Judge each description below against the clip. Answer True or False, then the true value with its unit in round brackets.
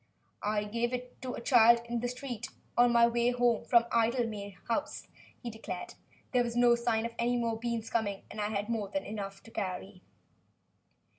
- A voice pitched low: False (235 Hz)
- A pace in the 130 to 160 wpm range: False (190 wpm)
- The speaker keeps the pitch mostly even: True (2.0 semitones)